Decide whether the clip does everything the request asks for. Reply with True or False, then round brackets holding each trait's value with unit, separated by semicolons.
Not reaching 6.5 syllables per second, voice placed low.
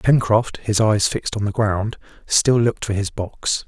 True (4.5 syllables/s; 105 Hz)